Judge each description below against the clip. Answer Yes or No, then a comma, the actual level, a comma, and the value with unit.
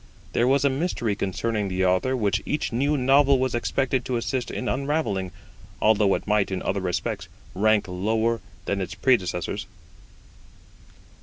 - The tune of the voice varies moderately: Yes, average, 5.0 semitones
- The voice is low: Yes, low, 115 Hz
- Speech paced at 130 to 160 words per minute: Yes, average, 150 wpm